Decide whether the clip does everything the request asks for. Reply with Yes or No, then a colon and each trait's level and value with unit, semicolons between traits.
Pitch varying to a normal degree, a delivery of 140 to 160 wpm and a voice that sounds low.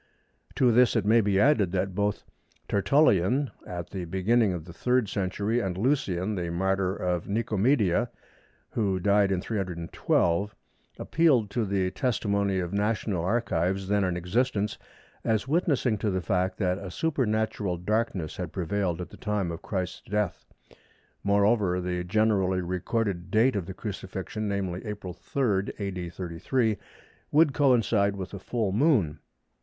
Yes: average, 3.4 semitones; average, 145 wpm; low, 100 Hz